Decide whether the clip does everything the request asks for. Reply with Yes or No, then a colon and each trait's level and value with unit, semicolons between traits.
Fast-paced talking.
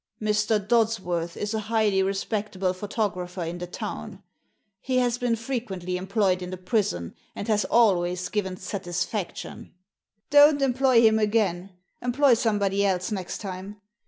No: average, 150 wpm